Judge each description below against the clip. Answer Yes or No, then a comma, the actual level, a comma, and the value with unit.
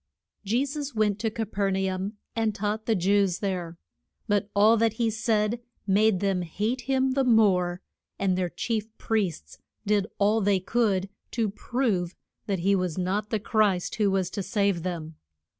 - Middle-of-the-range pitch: No, high, 205 Hz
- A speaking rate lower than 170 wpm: No, average, 175 wpm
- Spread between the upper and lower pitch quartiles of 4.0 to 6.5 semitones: No, average, 2.9 semitones